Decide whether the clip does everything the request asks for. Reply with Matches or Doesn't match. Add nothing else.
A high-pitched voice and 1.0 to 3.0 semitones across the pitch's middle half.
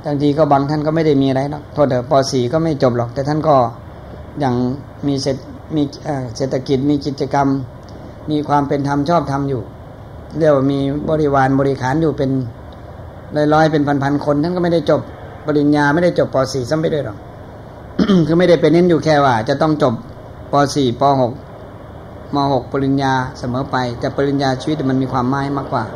Doesn't match